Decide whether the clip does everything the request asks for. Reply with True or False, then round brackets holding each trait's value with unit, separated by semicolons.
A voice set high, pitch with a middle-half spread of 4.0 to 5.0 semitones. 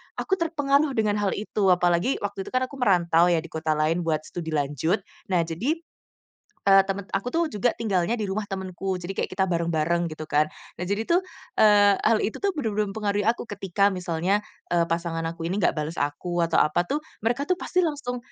True (195 Hz; 4.6 semitones)